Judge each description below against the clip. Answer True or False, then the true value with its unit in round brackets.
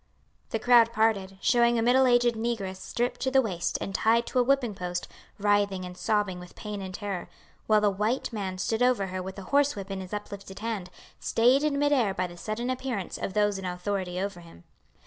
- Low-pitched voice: False (210 Hz)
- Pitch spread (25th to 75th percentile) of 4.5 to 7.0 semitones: False (4.1 semitones)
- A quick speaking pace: True (215 wpm)